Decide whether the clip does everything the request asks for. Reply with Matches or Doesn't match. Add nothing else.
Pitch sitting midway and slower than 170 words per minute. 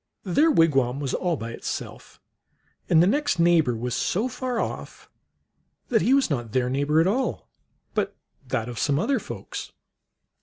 Doesn't match